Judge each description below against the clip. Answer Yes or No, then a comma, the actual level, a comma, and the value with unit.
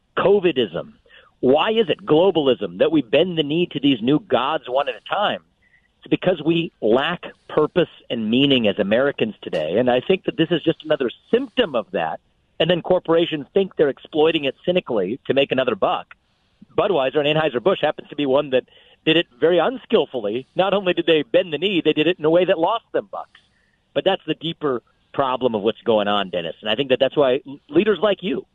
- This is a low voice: No, medium, 160 Hz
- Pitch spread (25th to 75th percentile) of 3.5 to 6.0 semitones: Yes, average, 4.5 semitones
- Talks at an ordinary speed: No, fast, 210 wpm